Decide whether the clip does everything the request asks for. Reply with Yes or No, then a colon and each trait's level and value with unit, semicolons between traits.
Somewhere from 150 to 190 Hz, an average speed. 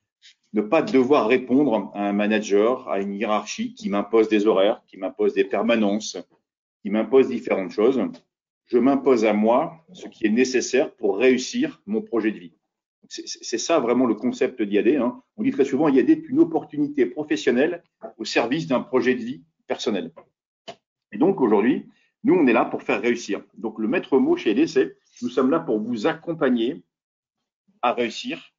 No: medium, 140 Hz; average, 180 wpm